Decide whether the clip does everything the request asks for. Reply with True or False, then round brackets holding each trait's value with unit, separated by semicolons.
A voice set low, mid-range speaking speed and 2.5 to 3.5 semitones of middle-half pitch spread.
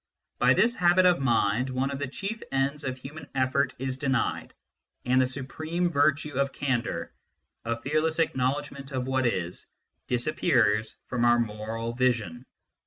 True (130 Hz; 150 wpm; 3.0 semitones)